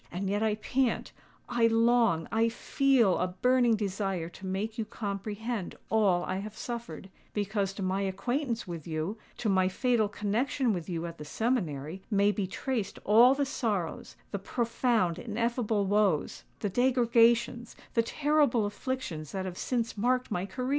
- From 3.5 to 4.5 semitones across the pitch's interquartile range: Yes, average, 3.9 semitones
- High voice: Yes, high, 215 Hz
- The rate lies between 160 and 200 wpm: No, slow, 135 wpm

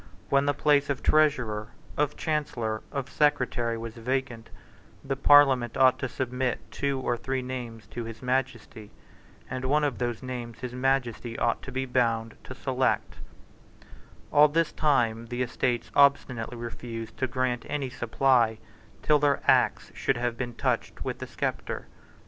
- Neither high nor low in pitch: No, low, 125 Hz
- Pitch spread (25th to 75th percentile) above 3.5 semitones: No, narrow, 2.6 semitones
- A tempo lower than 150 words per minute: No, average, 155 wpm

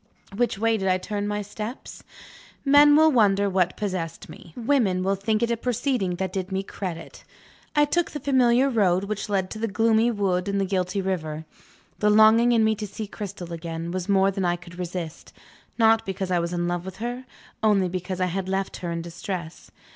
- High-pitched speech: Yes, high, 195 Hz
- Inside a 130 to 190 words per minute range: No, fast, 205 wpm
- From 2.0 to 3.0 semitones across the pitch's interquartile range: No, average, 3.5 semitones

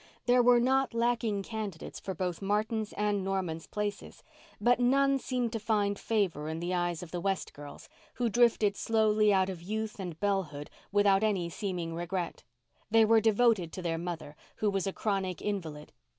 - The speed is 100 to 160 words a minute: No, average, 175 wpm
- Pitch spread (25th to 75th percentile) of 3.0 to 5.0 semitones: Yes, average, 3.9 semitones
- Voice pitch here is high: Yes, high, 200 Hz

